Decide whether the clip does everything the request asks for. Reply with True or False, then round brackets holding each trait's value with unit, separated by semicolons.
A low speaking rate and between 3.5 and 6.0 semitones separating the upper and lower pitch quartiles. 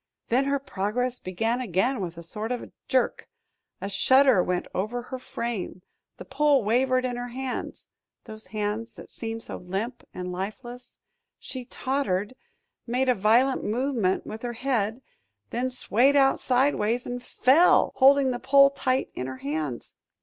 False (155 wpm; 4.0 semitones)